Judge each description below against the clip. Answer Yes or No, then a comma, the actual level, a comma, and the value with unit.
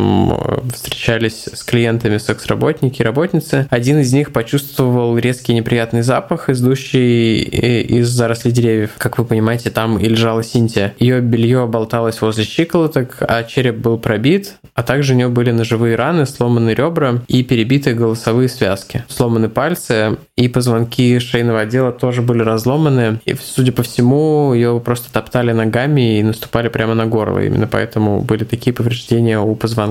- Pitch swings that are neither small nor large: No, narrow, 2.2 semitones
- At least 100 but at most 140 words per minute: No, average, 150 wpm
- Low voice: Yes, low, 120 Hz